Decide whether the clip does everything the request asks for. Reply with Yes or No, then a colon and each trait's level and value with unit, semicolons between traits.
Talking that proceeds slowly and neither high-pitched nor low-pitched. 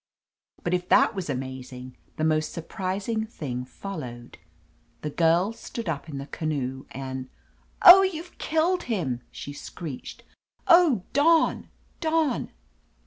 Yes: slow, 130 wpm; medium, 170 Hz